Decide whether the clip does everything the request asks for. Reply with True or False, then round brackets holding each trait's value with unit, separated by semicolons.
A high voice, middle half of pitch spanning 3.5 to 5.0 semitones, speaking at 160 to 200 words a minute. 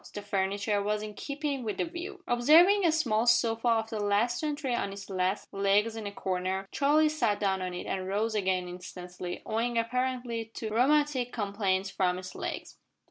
True (220 Hz; 4.3 semitones; 185 wpm)